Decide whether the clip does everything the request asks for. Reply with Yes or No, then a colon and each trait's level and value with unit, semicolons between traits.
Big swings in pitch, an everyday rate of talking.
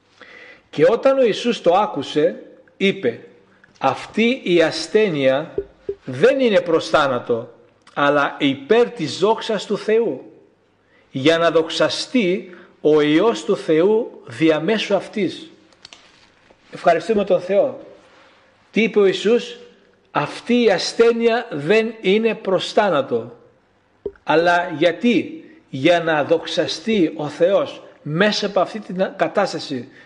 No: wide, 6.1 semitones; slow, 110 wpm